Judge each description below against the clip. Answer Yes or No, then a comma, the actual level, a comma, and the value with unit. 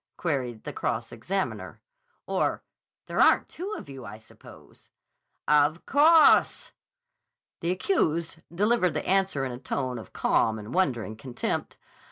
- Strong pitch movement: Yes, wide, 7.5 semitones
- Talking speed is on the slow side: Yes, slow, 130 wpm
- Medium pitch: Yes, medium, 150 Hz